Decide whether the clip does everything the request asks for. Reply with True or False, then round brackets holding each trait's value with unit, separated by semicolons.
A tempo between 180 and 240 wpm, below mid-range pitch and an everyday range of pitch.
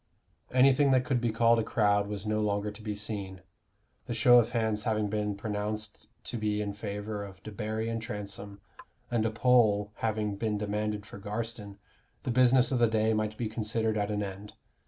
False (190 wpm; 110 Hz; 1.7 semitones)